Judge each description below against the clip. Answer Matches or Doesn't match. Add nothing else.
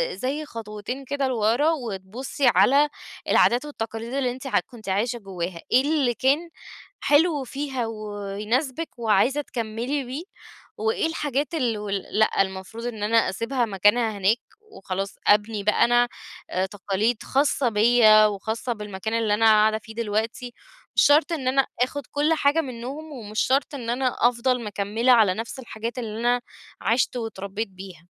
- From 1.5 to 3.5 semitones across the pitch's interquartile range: Doesn't match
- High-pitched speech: Matches